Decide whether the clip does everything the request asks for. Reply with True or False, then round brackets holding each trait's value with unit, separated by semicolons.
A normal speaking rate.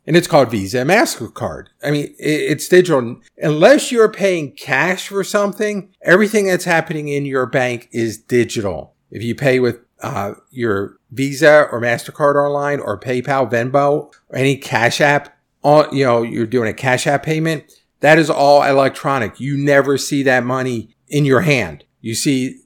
True (170 wpm)